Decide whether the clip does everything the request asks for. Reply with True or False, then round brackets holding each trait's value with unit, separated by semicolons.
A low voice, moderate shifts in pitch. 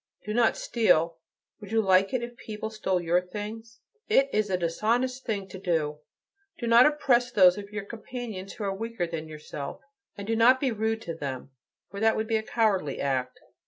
False (210 Hz; 4.3 semitones)